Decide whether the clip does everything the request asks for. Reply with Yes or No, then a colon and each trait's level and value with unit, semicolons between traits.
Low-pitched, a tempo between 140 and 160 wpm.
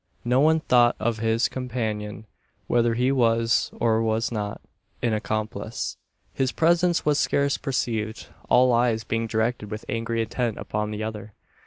Yes: low, 115 Hz; average, 150 wpm